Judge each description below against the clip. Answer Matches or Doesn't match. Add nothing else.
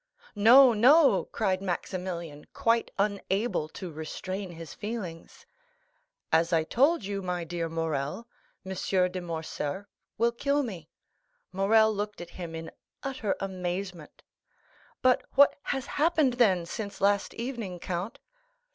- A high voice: Matches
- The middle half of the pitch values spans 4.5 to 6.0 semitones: Matches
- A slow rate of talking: Matches